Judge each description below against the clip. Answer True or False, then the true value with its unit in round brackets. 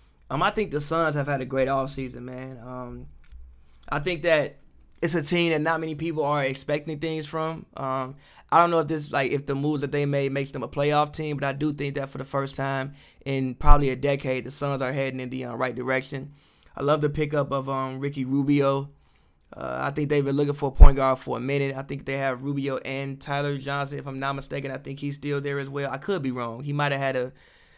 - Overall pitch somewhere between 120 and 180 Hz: True (140 Hz)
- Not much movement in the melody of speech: True (1.6 semitones)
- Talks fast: True (250 wpm)